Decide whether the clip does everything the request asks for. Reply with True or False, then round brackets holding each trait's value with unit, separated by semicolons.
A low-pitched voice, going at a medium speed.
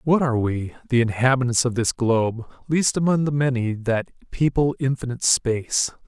True (130 Hz; 160 wpm)